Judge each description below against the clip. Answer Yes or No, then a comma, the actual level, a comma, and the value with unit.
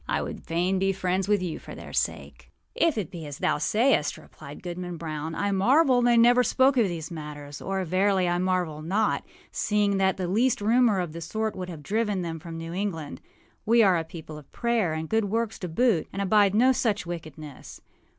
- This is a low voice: No, medium, 185 Hz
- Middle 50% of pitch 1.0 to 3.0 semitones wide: No, average, 4.8 semitones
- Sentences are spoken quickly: Yes, fast, 210 wpm